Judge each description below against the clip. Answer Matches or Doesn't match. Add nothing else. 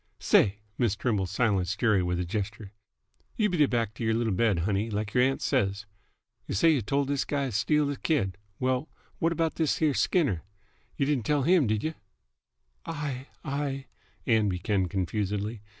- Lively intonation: Matches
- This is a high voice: Doesn't match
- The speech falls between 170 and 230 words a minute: Matches